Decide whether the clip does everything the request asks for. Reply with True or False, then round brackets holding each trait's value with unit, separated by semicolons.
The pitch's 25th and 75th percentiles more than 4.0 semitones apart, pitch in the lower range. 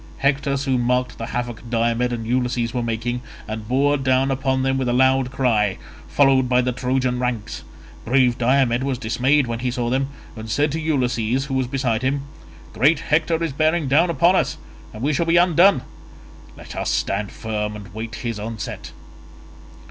False (2.6 semitones; 125 Hz)